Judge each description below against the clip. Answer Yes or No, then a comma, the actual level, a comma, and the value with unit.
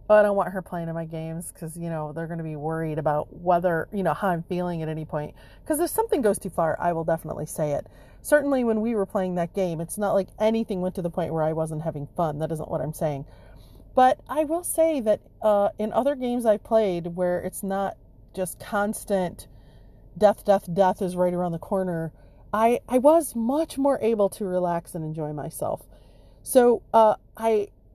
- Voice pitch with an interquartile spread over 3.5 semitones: Yes, average, 4.9 semitones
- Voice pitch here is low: No, medium, 185 Hz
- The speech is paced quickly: Yes, fast, 215 wpm